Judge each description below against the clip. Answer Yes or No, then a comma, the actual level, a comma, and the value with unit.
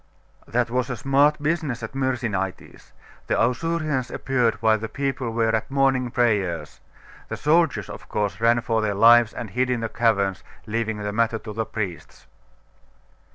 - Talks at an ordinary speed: Yes, average, 160 wpm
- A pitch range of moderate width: Yes, average, 3.3 semitones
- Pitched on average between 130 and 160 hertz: No, low, 115 Hz